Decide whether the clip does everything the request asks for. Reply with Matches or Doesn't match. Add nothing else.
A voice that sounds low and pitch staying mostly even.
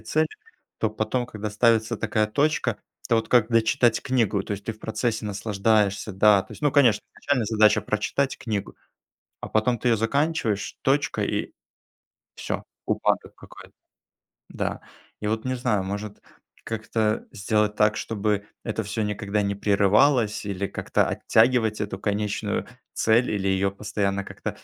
Matches